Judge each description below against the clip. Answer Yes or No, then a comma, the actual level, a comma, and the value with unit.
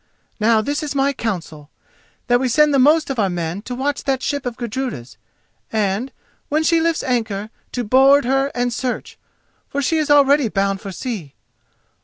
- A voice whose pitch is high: Yes, very high, 250 Hz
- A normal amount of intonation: Yes, average, 5.0 semitones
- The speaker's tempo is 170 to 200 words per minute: Yes, average, 180 wpm